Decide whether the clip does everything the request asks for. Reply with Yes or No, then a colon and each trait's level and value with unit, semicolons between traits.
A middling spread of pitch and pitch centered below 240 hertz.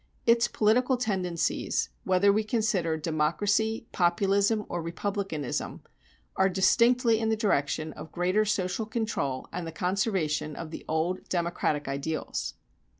Yes: average, 4.9 semitones; high, 190 Hz